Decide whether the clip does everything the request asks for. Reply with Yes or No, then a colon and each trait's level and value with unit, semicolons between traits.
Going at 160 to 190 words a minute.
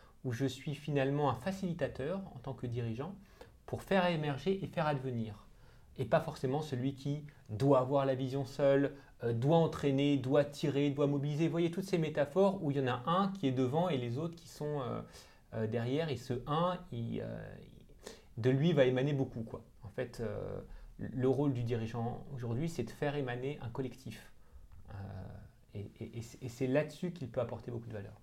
No: average, 200 wpm